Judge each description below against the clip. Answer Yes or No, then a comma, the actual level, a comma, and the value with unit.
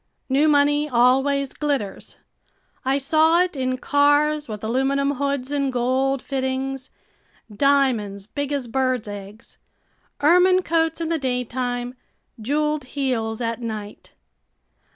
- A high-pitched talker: Yes, very high, 270 Hz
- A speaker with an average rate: No, slow, 115 wpm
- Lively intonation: No, average, 2.9 semitones